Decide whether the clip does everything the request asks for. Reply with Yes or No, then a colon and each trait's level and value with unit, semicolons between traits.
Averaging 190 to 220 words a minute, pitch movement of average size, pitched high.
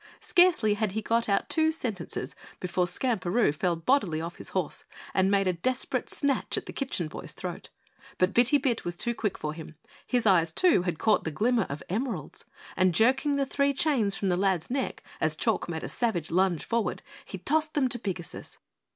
No: average, 195 wpm; wide, 6.4 semitones; high, 205 Hz